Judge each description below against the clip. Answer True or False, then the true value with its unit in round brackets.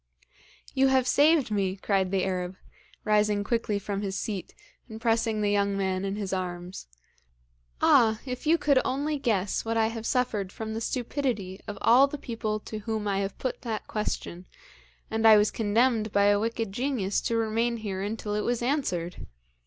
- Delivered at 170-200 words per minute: True (180 wpm)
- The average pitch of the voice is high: True (215 Hz)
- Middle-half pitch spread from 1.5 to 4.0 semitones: True (3.0 semitones)